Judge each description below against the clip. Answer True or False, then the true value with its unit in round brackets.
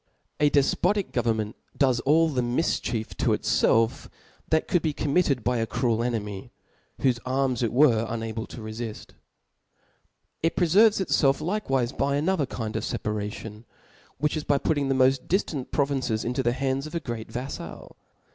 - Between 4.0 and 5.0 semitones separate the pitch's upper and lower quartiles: True (4.4 semitones)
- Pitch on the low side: True (130 Hz)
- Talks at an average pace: True (155 wpm)